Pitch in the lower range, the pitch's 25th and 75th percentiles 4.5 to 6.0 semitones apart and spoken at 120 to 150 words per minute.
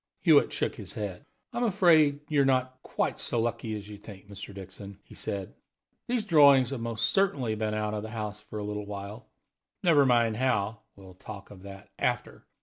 No: low, 110 Hz; average, 4.8 semitones; average, 190 wpm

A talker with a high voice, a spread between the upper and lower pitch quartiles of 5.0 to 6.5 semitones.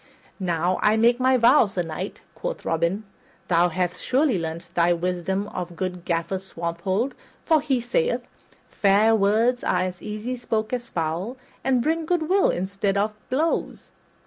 Yes: high, 200 Hz; wide, 5.6 semitones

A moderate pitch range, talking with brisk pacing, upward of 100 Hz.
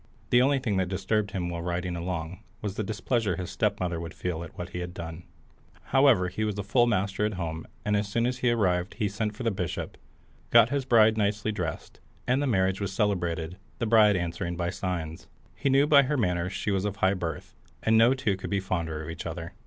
No: average, 3.9 semitones; fast, 225 wpm; very low, 95 Hz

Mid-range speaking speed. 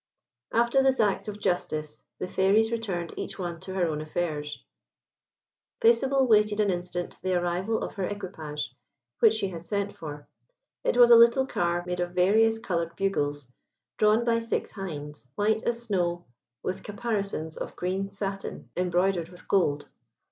Yes: average, 155 wpm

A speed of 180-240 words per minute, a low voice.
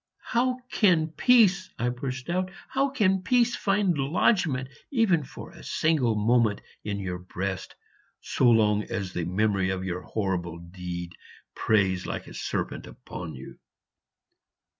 No: average, 140 wpm; low, 120 Hz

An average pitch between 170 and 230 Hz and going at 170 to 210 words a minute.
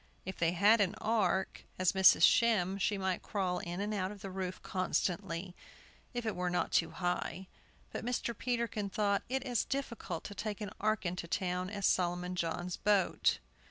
Yes: high, 190 Hz; average, 180 wpm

